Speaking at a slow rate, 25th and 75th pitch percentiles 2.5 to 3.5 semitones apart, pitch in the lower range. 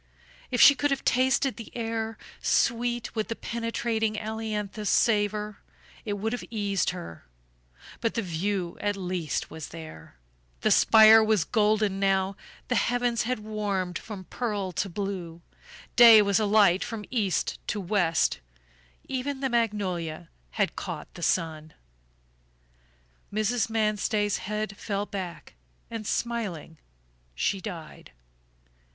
No: slow, 125 wpm; average, 3.2 semitones; high, 210 Hz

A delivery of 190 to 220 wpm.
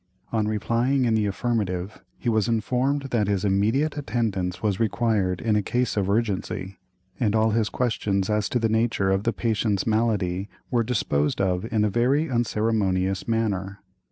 No: average, 165 wpm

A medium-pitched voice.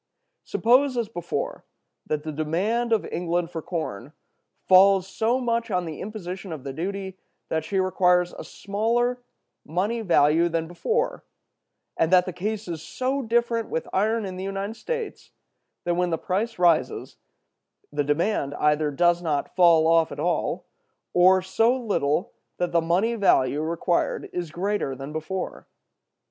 Yes: medium, 180 Hz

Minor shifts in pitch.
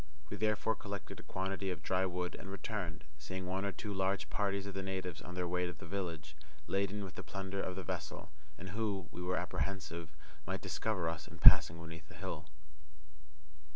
Yes: narrow, 2.3 semitones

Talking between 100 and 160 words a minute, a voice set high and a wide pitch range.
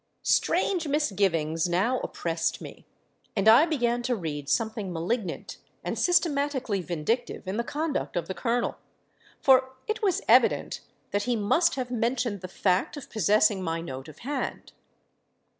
Yes: average, 145 wpm; high, 225 Hz; wide, 6.4 semitones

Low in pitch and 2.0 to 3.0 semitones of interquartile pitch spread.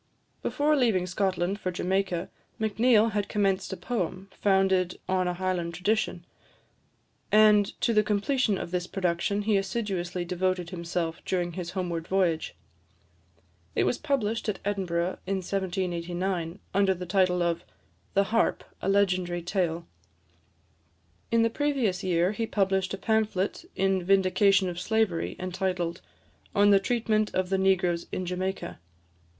No: high, 190 Hz; narrow, 2.4 semitones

